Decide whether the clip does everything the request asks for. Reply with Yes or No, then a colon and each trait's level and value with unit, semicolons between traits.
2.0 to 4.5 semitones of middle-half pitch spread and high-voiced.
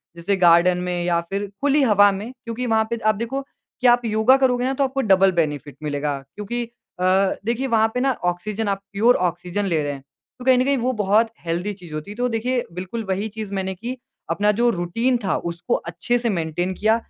No: average, 5.1 semitones; high, 205 Hz